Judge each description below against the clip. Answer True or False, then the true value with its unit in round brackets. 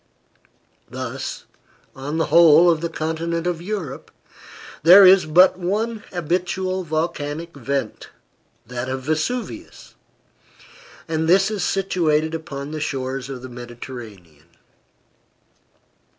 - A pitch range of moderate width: True (4.7 semitones)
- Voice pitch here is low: False (160 Hz)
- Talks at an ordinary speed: False (110 wpm)